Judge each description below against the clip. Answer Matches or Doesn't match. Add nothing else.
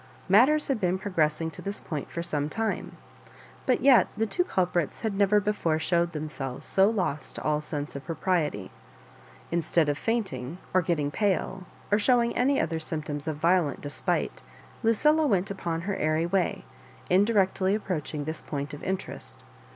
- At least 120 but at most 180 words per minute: Matches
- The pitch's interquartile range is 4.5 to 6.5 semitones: Matches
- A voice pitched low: Doesn't match